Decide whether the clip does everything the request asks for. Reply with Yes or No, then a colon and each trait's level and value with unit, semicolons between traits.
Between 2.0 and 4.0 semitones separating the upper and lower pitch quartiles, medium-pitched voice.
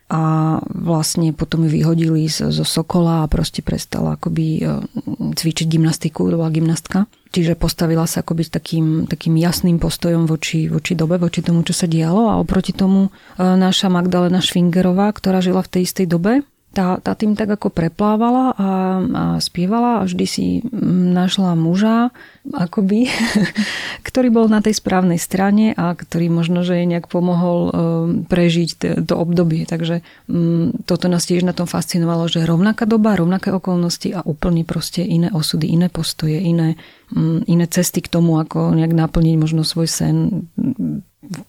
Yes: narrow, 2.5 semitones; medium, 175 Hz